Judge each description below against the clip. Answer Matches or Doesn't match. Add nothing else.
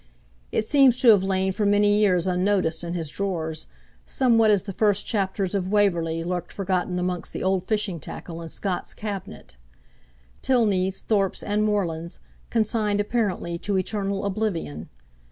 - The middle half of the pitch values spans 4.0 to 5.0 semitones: Doesn't match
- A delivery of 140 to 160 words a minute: Matches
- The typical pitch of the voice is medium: Doesn't match